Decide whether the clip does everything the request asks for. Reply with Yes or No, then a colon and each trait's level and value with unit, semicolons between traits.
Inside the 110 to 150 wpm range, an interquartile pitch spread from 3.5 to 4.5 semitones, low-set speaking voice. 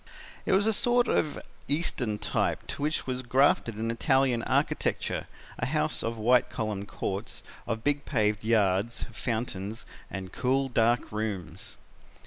Yes: average, 140 wpm; average, 4.0 semitones; low, 115 Hz